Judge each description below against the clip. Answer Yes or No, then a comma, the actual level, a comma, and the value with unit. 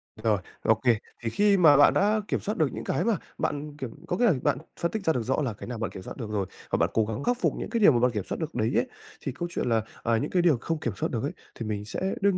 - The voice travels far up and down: Yes, wide, 7.5 semitones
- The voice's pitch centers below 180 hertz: Yes, low, 135 Hz